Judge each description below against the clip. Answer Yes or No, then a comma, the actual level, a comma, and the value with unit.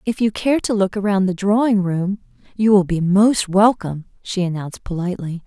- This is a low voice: No, high, 195 Hz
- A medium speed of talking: Yes, average, 185 wpm